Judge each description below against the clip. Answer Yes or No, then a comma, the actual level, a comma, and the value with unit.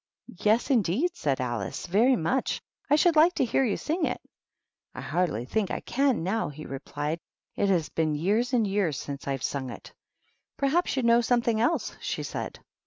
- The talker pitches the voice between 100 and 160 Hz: No, high, 205 Hz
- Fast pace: No, average, 195 wpm